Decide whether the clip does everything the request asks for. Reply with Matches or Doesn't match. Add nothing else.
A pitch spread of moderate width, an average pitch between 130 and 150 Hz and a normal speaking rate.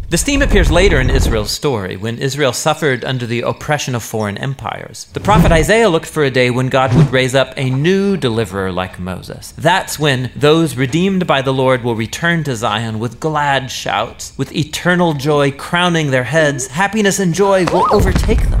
Matches